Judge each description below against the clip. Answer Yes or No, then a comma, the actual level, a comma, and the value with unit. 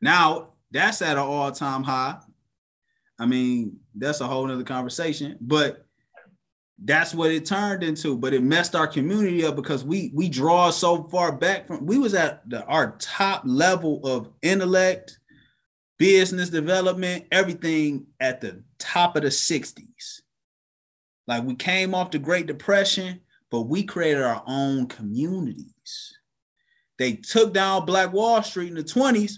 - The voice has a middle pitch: Yes, medium, 170 Hz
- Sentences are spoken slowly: No, average, 150 wpm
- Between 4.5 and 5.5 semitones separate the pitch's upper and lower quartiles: Yes, average, 5.0 semitones